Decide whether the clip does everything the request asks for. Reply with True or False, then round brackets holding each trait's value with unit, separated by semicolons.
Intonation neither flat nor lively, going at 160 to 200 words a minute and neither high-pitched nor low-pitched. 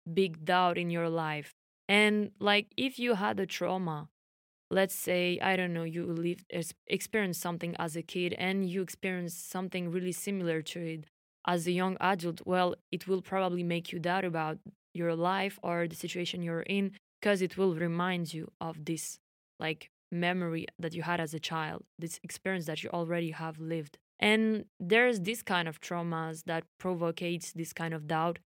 False (2.3 semitones; 180 wpm; 175 Hz)